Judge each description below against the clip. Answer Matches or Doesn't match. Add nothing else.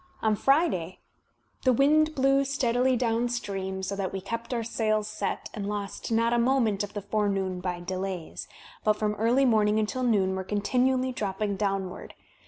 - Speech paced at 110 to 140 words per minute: Doesn't match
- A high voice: Matches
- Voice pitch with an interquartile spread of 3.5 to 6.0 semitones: Matches